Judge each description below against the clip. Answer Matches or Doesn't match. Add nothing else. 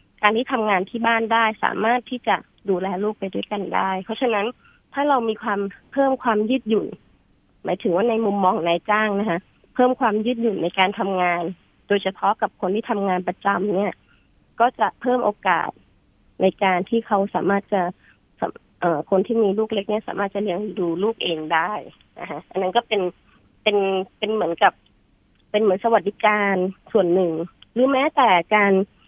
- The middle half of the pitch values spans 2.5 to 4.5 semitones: Matches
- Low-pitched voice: Doesn't match